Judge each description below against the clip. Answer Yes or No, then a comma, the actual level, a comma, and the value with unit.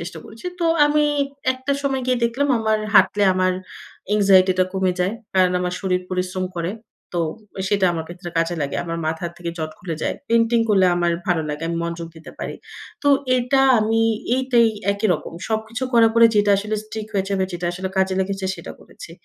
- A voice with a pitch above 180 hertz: Yes, high, 190 Hz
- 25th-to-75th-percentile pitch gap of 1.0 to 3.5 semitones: No, average, 4.1 semitones